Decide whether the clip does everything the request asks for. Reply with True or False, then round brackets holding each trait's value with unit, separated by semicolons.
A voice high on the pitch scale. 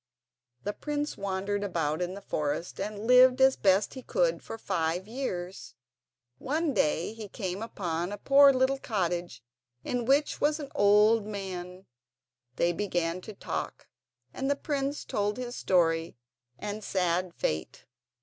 True (205 Hz)